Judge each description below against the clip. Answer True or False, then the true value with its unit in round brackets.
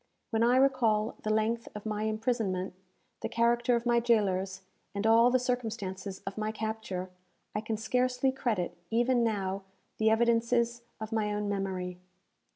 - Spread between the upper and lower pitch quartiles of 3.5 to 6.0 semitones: False (2.7 semitones)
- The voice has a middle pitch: False (220 Hz)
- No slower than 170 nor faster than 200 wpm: False (155 wpm)